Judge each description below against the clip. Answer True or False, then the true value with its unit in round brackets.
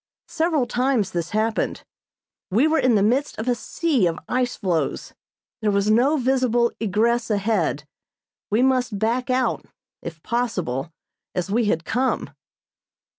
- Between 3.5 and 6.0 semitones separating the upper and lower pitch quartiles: True (4.1 semitones)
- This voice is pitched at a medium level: False (230 Hz)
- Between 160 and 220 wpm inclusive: False (140 wpm)